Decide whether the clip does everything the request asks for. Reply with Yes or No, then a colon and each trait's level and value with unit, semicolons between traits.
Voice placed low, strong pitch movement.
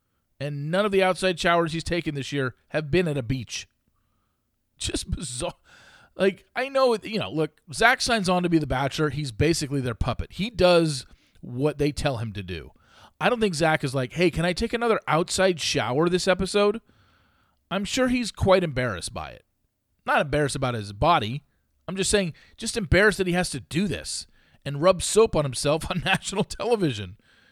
No: medium, 160 Hz; wide, 6.0 semitones